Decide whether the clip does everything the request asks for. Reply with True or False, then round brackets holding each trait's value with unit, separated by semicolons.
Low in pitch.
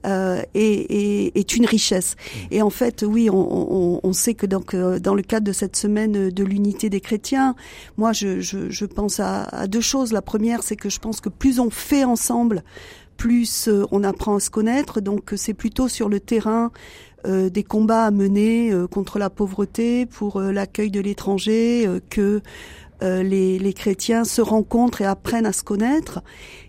False (210 Hz)